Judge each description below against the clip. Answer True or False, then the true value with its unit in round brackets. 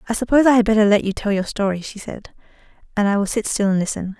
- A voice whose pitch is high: True (210 Hz)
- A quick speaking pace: True (270 wpm)